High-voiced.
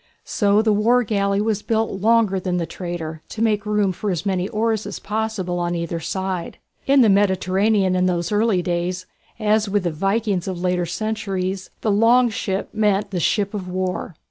Yes: high, 195 Hz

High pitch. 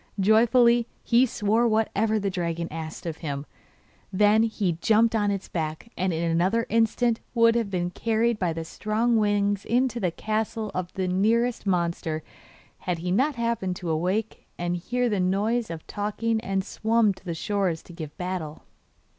Yes: high, 205 Hz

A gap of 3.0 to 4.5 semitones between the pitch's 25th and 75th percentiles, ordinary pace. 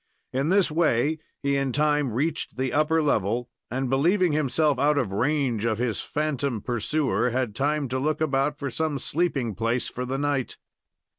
Yes: average, 3.5 semitones; average, 170 wpm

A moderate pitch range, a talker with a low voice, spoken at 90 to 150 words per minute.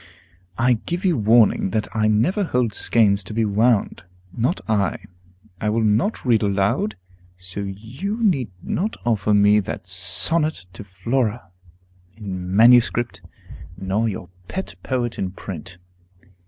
Yes: average, 3.8 semitones; low, 110 Hz; slow, 135 wpm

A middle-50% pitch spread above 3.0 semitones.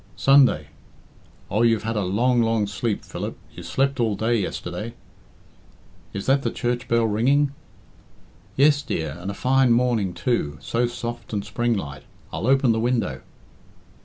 Yes: average, 3.7 semitones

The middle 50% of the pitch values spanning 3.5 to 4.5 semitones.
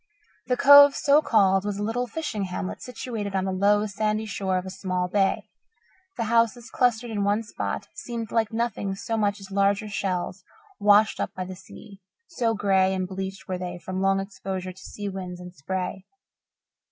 No: average, 3.0 semitones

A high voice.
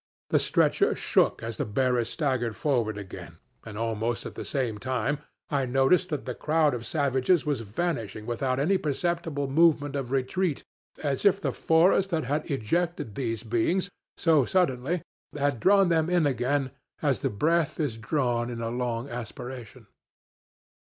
No: low, 135 Hz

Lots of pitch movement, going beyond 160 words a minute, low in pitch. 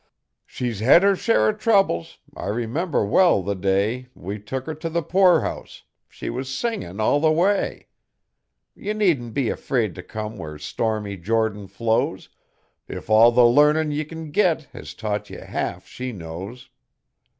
No: wide, 7.4 semitones; average, 155 wpm; low, 120 Hz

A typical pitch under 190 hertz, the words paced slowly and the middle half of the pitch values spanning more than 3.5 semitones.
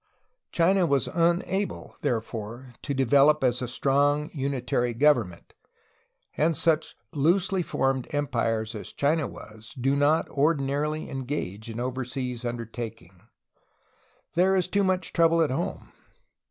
Yes: medium, 140 Hz; slow, 125 wpm; average, 4.7 semitones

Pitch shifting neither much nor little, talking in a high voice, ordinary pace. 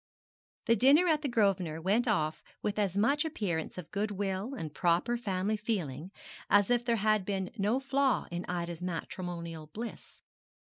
Yes: average, 4.9 semitones; high, 200 Hz; average, 155 wpm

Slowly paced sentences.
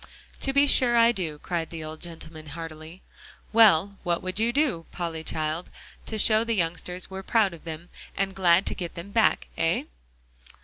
No: average, 180 wpm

